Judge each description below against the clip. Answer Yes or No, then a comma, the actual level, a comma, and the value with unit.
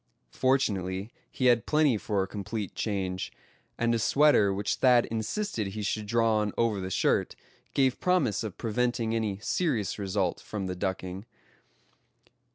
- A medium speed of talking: Yes, average, 150 wpm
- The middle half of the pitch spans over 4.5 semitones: No, average, 3.6 semitones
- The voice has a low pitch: Yes, low, 110 Hz